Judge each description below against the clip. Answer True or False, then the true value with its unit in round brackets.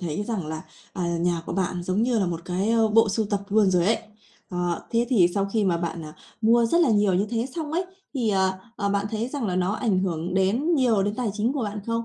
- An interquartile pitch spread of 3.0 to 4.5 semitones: True (4.1 semitones)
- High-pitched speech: True (205 Hz)